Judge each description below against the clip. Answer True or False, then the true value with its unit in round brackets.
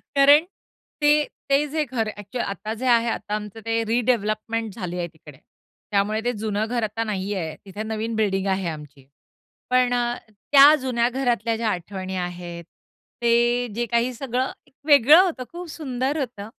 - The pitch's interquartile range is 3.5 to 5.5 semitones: True (3.9 semitones)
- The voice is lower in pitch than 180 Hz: False (225 Hz)